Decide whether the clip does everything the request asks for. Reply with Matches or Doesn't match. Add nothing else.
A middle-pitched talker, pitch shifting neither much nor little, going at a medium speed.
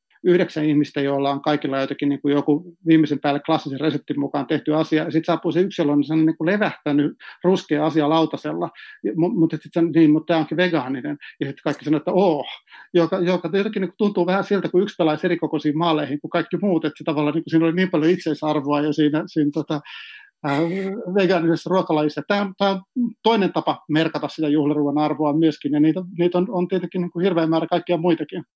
Doesn't match